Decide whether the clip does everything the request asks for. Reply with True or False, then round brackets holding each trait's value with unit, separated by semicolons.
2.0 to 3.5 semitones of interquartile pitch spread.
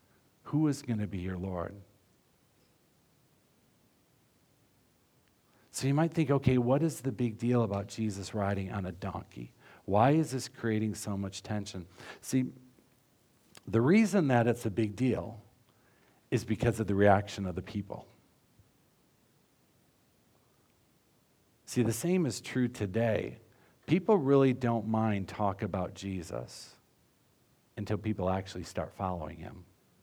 False (4.3 semitones)